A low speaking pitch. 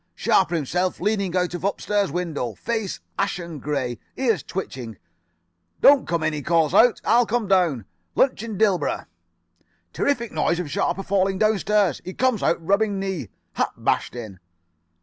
No: medium, 185 Hz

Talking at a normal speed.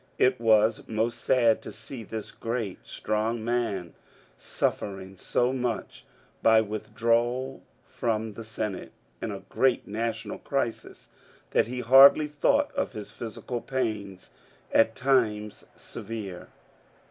No: slow, 120 wpm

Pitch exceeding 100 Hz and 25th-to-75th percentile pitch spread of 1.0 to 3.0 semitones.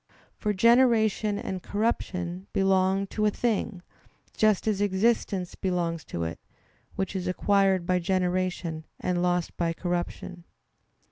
Yes: high, 190 Hz; narrow, 2.5 semitones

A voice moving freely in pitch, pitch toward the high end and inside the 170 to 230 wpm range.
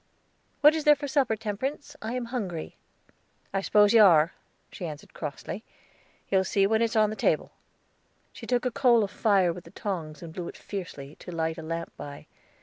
Yes: wide, 5.8 semitones; high, 200 Hz; average, 195 wpm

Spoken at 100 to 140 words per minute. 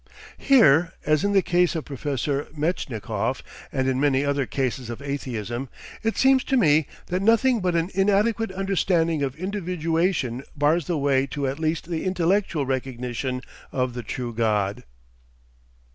No: average, 150 wpm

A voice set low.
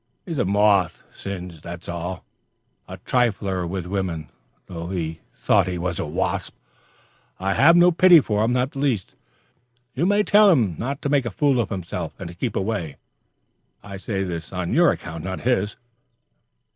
Yes: low, 100 Hz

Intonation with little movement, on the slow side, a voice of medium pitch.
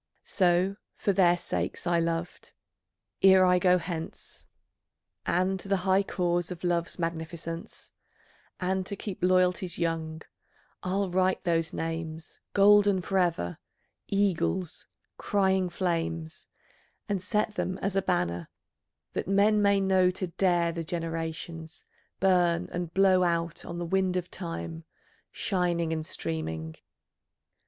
Yes: narrow, 2.3 semitones; slow, 125 wpm; medium, 180 Hz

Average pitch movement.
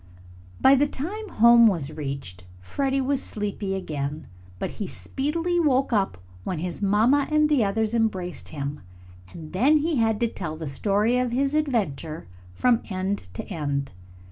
No: wide, 8.6 semitones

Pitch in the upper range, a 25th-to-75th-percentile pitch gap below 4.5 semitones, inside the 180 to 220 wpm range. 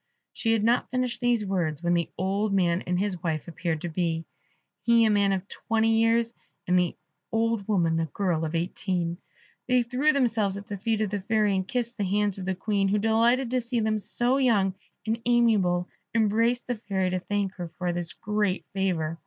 Yes: high, 205 Hz; average, 4.0 semitones; average, 200 wpm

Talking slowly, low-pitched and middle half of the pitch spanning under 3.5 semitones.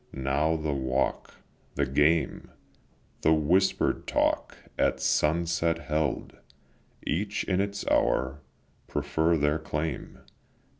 Yes: slow, 100 wpm; very low, 80 Hz; narrow, 2.4 semitones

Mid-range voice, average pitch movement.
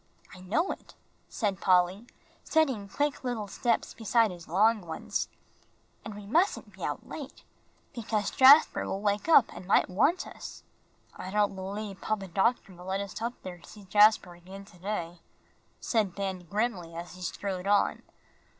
No: high, 200 Hz; average, 3.3 semitones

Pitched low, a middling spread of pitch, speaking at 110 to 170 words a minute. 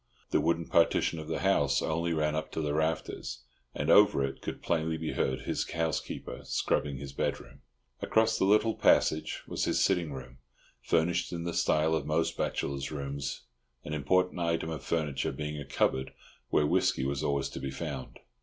No: very low, 80 Hz; average, 3.1 semitones; average, 180 wpm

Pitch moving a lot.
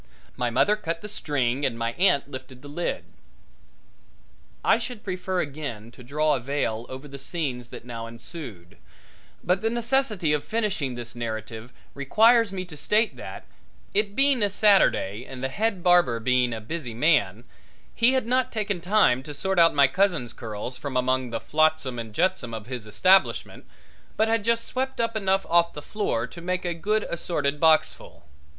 Yes: wide, 8.1 semitones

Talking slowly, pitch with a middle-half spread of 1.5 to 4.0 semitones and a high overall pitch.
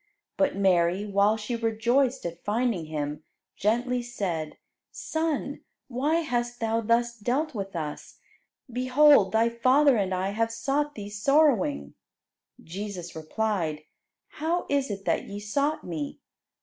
No: slow, 130 wpm; average, 5.0 semitones; high, 225 Hz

